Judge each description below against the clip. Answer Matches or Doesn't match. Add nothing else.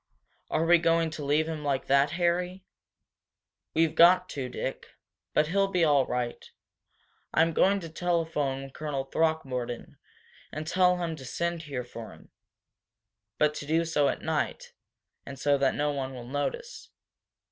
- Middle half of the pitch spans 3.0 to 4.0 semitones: Matches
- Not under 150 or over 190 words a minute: Matches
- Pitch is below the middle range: Doesn't match